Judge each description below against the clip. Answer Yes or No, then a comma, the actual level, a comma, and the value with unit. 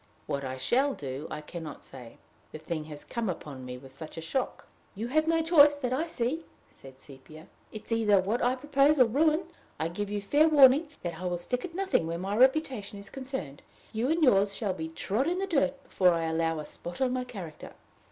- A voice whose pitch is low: No, high, 205 Hz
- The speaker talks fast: Yes, fast, 225 wpm